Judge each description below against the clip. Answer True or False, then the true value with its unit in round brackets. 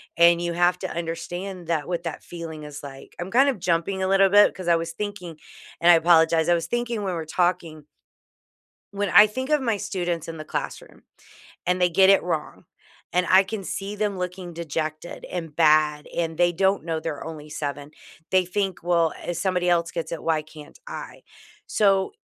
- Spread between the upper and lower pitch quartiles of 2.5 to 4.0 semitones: True (2.8 semitones)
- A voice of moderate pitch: True (175 Hz)